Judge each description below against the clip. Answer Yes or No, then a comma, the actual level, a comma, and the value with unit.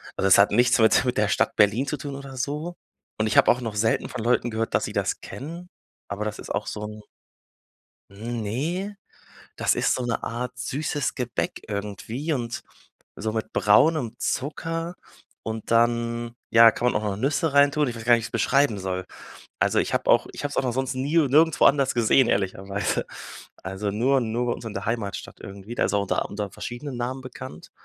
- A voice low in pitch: Yes, low, 120 Hz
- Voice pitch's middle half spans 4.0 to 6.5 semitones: Yes, average, 4.4 semitones